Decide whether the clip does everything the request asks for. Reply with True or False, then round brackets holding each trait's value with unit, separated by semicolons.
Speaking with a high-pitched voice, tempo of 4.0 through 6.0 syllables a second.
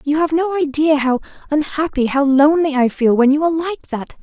True (295 Hz; 5.8 syllables/s)